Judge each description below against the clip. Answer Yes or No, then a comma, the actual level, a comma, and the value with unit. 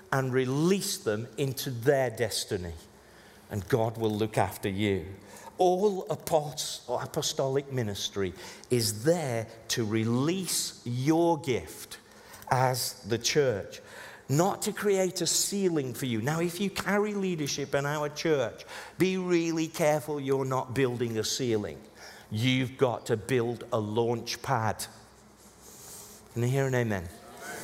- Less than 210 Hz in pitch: Yes, low, 135 Hz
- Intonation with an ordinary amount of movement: No, wide, 6.7 semitones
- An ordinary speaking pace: No, slow, 130 wpm